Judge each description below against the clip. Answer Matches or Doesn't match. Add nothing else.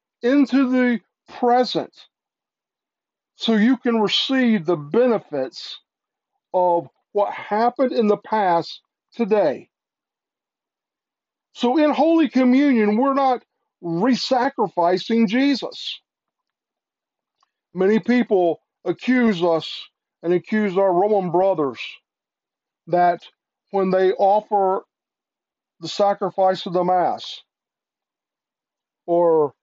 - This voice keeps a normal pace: Doesn't match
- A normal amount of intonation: Doesn't match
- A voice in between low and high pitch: Doesn't match